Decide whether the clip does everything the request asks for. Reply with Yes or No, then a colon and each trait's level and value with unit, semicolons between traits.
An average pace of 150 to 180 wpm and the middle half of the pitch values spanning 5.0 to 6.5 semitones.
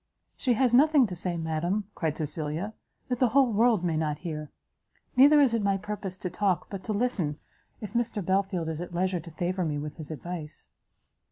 No: average, 195 wpm; wide, 5.6 semitones